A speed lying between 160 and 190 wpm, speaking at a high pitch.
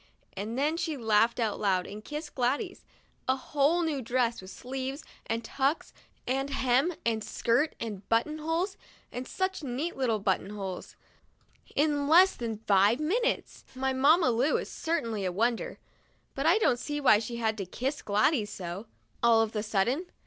Yes: average, 170 wpm; very high, 250 Hz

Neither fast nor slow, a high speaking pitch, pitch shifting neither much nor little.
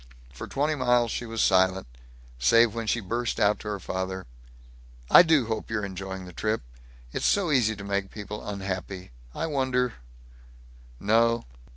No: average, 160 wpm; low, 110 Hz; average, 3.9 semitones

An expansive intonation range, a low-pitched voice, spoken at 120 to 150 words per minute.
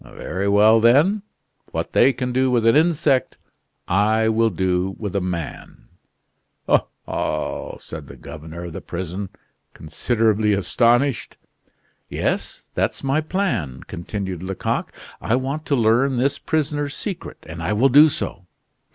Yes: wide, 6.4 semitones; low, 110 Hz; average, 140 wpm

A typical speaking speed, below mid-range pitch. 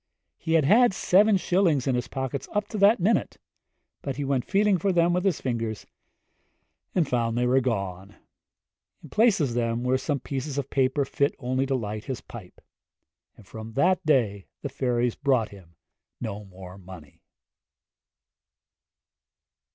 Yes: average, 160 wpm; low, 130 Hz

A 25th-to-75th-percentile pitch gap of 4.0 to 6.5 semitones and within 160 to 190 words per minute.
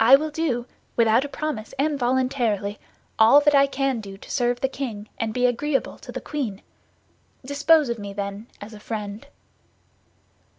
Yes: average, 4.5 semitones; average, 170 wpm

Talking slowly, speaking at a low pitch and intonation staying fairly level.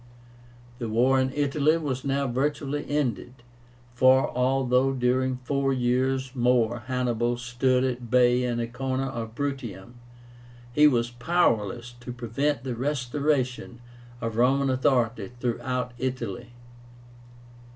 Yes: slow, 120 wpm; low, 125 Hz; narrow, 1.9 semitones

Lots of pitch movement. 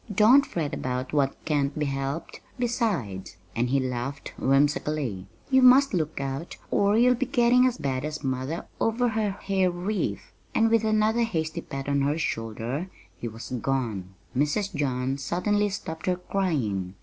Yes: wide, 7.9 semitones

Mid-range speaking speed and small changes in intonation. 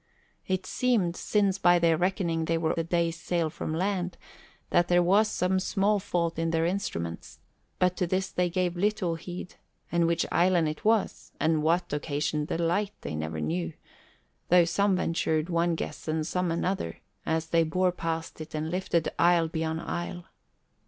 Yes: average, 175 wpm; narrow, 2.1 semitones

